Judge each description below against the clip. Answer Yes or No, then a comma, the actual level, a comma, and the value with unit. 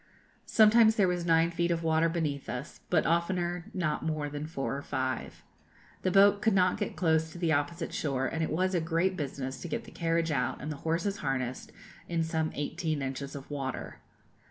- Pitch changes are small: No, average, 3.4 semitones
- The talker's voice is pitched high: No, medium, 165 Hz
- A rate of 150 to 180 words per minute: No, average, 200 wpm